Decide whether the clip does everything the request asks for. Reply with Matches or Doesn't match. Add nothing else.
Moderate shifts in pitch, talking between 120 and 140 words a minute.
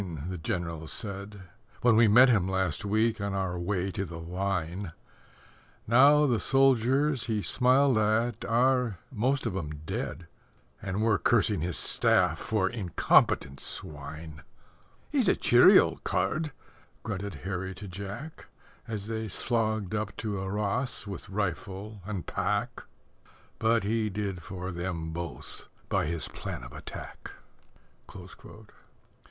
Matches